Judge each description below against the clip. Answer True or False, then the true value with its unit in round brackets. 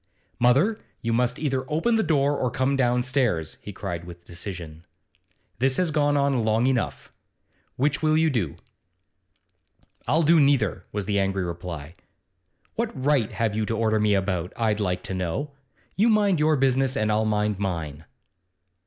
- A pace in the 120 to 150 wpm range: False (160 wpm)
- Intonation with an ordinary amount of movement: False (6.6 semitones)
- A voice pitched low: True (120 Hz)